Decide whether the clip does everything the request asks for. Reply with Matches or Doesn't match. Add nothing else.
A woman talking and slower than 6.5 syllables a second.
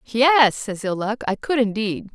Matches